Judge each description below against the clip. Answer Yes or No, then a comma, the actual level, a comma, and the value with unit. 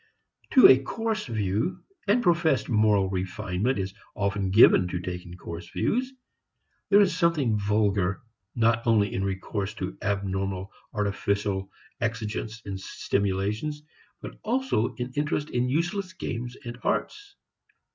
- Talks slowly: Yes, slow, 125 wpm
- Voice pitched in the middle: No, low, 110 Hz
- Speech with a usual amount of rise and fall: No, wide, 7.2 semitones